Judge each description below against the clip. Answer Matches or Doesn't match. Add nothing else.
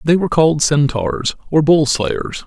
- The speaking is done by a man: Matches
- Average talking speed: Matches